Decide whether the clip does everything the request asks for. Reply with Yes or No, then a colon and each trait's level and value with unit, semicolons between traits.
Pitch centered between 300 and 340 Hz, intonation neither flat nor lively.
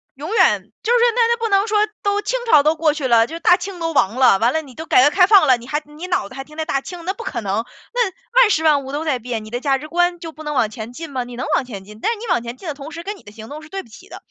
No: very high, 305 Hz; wide, 6.4 semitones